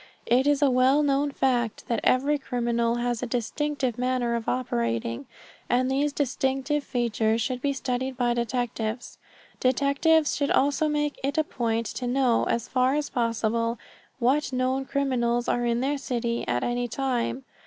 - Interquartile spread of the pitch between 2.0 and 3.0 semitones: Yes, average, 2.7 semitones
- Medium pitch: No, very high, 255 Hz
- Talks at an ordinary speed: Yes, average, 160 wpm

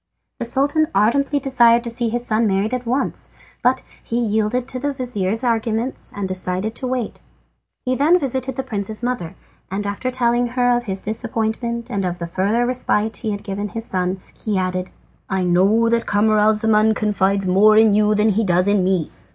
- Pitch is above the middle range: Yes, high, 220 Hz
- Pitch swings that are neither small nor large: Yes, average, 3.4 semitones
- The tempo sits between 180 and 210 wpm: Yes, average, 185 wpm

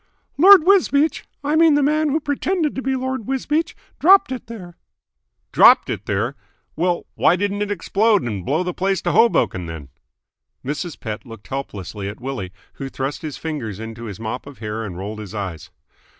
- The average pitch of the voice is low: No, medium, 160 Hz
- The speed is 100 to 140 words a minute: No, average, 180 wpm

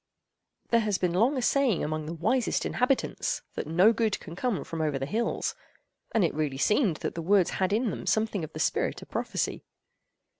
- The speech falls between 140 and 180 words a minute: No, average, 200 wpm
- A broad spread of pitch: Yes, wide, 5.9 semitones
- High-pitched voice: Yes, high, 195 Hz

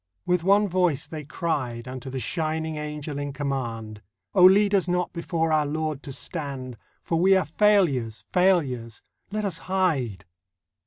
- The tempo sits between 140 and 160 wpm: Yes, average, 155 wpm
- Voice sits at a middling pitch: Yes, medium, 155 Hz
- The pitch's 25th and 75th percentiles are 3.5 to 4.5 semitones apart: No, average, 5.3 semitones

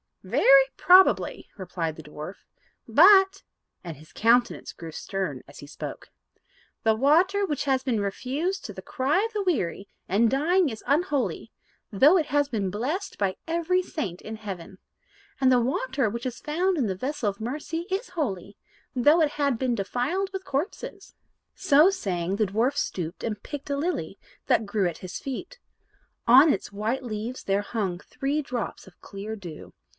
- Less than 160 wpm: No, average, 170 wpm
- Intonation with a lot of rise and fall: Yes, wide, 7.5 semitones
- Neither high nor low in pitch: No, very high, 255 Hz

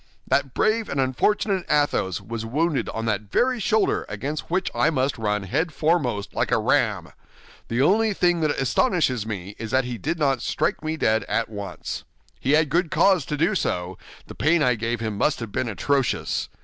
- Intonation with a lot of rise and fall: Yes, wide, 6.7 semitones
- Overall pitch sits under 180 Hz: Yes, low, 135 Hz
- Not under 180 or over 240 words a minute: Yes, average, 190 wpm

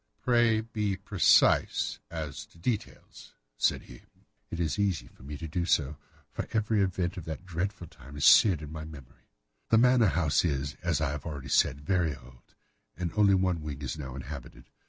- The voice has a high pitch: No, very low, 85 Hz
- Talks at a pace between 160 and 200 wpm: Yes, average, 185 wpm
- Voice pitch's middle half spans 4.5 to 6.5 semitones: Yes, average, 5.2 semitones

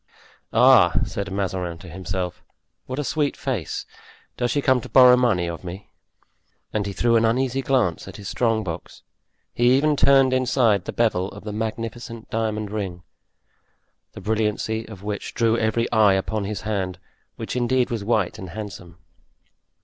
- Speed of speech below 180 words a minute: Yes, average, 165 wpm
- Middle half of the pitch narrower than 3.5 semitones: No, average, 3.9 semitones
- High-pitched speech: No, low, 110 Hz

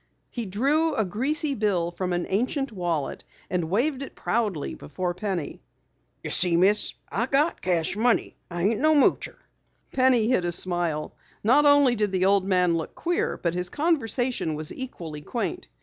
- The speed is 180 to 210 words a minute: No, average, 165 wpm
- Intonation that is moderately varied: No, wide, 6.8 semitones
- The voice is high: Yes, high, 205 Hz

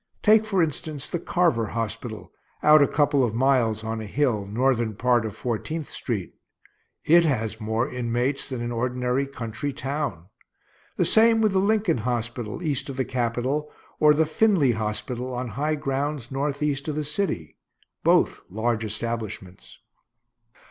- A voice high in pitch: No, low, 130 Hz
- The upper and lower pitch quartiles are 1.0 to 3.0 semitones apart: No, average, 4.5 semitones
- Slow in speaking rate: No, average, 150 wpm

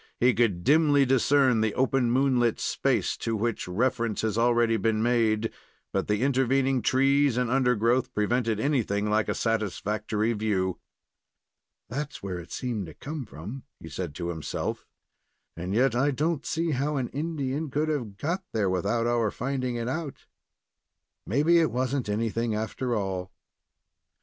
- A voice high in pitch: No, low, 120 Hz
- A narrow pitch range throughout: No, average, 4.1 semitones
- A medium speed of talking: Yes, average, 155 wpm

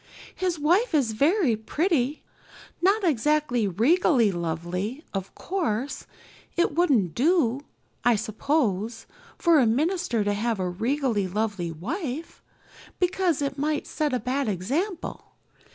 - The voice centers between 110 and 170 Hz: No, very high, 265 Hz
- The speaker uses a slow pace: Yes, slow, 120 wpm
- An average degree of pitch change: No, wide, 7.1 semitones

